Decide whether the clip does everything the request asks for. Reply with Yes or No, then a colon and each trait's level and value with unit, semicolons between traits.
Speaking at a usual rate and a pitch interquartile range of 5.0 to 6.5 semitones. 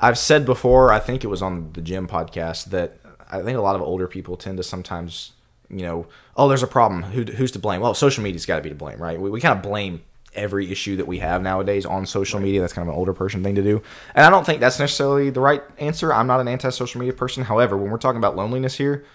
No: fast, 270 wpm; wide, 5.4 semitones